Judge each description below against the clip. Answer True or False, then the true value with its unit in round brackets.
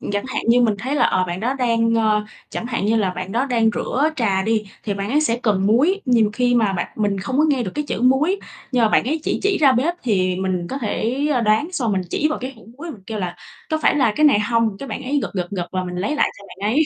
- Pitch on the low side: False (230 Hz)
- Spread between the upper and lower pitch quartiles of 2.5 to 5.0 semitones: True (4.7 semitones)